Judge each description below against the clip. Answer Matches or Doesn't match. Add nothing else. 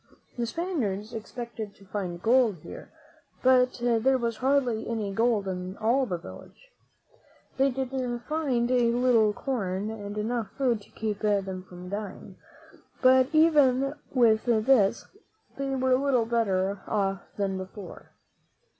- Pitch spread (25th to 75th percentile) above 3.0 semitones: Matches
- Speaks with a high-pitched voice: Matches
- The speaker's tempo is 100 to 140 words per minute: Matches